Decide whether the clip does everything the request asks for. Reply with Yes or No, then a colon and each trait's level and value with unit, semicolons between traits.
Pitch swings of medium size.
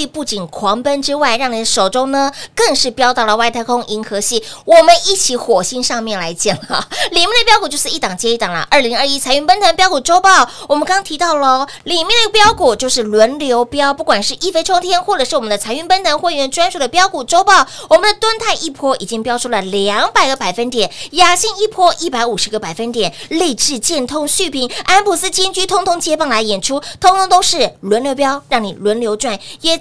No: wide, 7.2 semitones